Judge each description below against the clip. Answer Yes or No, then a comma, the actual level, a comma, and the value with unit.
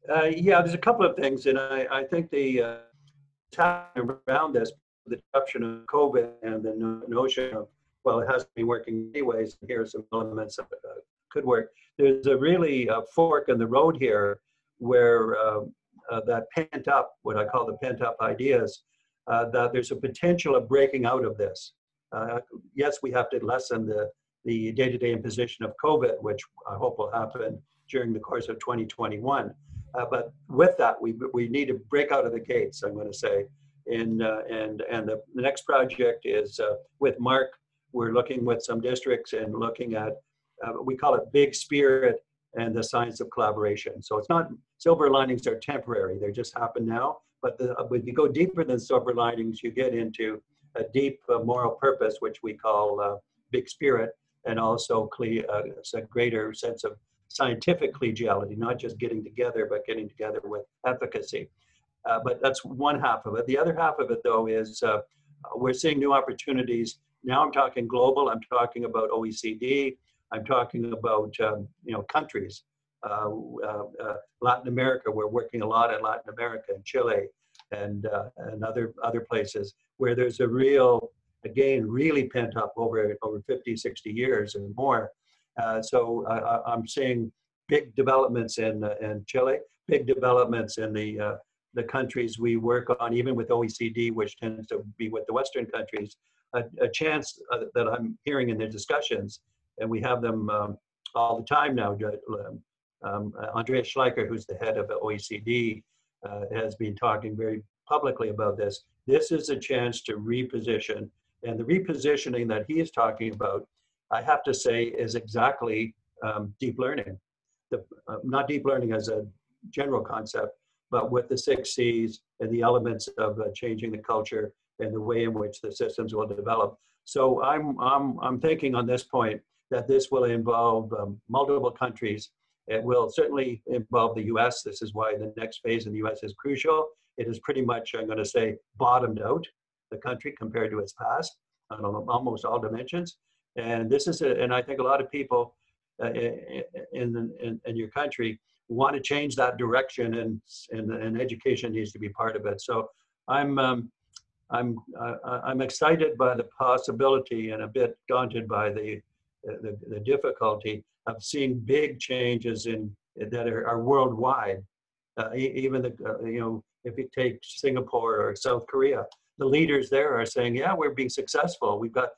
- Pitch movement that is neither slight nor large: Yes, average, 4.3 semitones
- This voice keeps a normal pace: Yes, average, 180 wpm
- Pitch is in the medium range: No, low, 125 Hz